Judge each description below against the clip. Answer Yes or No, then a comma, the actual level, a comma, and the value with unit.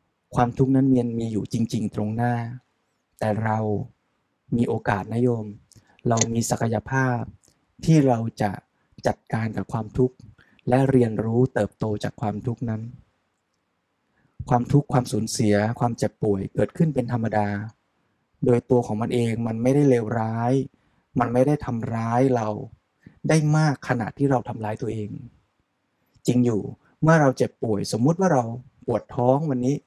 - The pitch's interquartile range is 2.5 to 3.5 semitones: Yes, average, 3.0 semitones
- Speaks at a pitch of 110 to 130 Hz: Yes, low, 120 Hz